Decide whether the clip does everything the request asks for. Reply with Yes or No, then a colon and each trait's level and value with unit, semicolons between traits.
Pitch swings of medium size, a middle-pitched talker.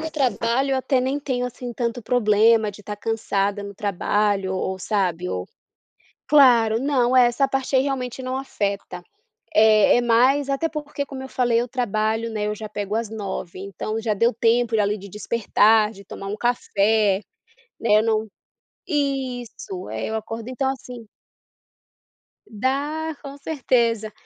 No: average, 3.7 semitones; high, 230 Hz